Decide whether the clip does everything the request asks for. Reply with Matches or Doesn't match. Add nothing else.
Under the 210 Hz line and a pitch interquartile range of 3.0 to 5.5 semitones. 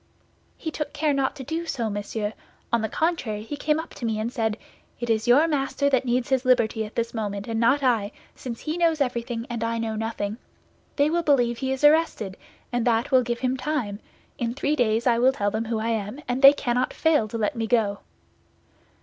Doesn't match